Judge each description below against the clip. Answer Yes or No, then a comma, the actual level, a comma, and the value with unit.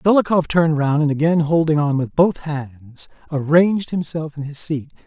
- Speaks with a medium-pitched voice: Yes, medium, 155 Hz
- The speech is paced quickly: No, average, 180 wpm